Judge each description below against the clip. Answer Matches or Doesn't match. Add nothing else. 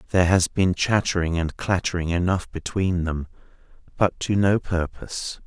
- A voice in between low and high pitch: Doesn't match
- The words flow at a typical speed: Matches